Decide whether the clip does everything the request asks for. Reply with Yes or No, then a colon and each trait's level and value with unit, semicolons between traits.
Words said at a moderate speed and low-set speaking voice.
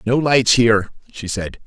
Yes: average, 180 wpm; low, 115 Hz